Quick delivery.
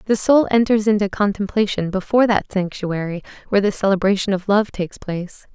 No: average, 160 wpm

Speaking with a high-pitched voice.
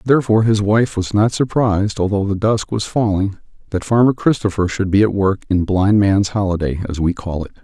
No: low, 100 Hz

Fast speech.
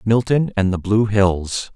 No: average, 170 wpm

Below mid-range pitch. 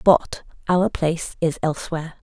No: medium, 165 Hz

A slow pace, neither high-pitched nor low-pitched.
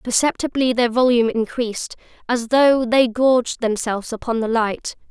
No: slow, 130 wpm; high, 240 Hz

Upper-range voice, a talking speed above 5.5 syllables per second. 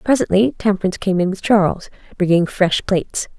Yes: high, 195 Hz; 5.8 syllables/s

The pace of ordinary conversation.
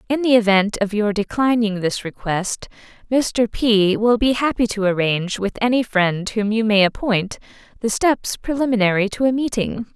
Yes: average, 170 wpm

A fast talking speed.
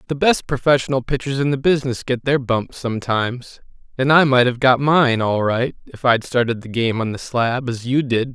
Yes: fast, 215 wpm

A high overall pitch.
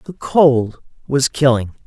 No: medium, 140 Hz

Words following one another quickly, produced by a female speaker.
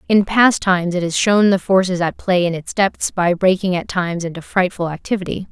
Yes: fast, 220 wpm; female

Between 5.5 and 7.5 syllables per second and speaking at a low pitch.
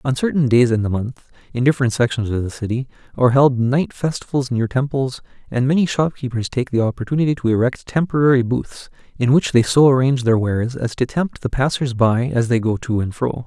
Yes: 5.8 syllables/s; low, 125 Hz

